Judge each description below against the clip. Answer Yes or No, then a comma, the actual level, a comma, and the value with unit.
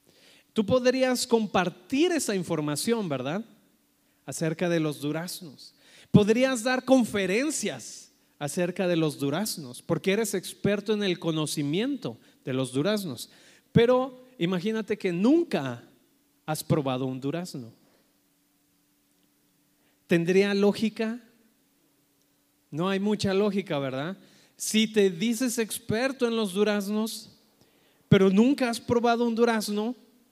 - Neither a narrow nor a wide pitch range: No, wide, 6.0 semitones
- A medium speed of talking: No, slow, 105 wpm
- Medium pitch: No, high, 205 Hz